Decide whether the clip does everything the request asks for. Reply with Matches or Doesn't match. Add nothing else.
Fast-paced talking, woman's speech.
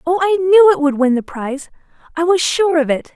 Matches